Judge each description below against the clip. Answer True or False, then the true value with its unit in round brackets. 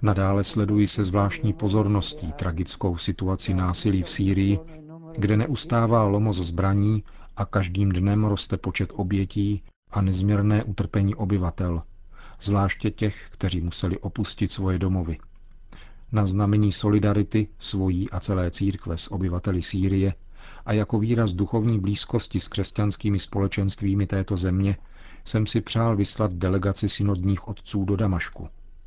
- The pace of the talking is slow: False (125 wpm)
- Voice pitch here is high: False (100 Hz)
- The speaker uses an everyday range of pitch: False (1.9 semitones)